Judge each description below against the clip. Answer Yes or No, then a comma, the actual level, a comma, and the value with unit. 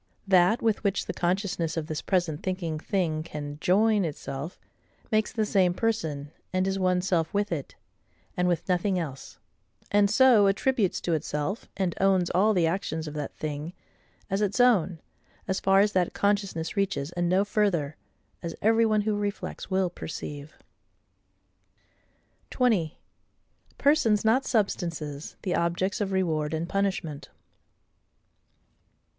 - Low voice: No, medium, 185 Hz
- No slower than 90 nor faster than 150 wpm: Yes, average, 140 wpm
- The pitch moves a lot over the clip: No, average, 4.0 semitones